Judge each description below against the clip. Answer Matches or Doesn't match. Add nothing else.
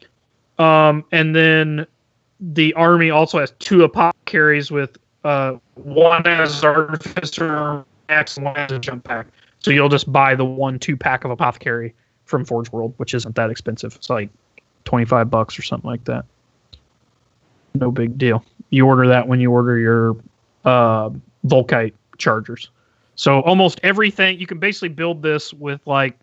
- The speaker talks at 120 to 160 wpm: Matches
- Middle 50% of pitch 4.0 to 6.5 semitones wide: Matches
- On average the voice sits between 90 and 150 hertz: Matches